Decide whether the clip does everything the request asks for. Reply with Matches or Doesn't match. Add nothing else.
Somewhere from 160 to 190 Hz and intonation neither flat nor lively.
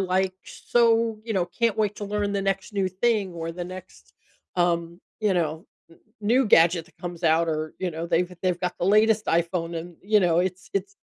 Matches